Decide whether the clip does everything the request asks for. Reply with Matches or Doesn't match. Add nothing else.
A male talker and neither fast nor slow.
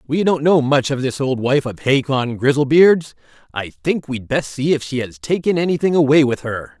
Doesn't match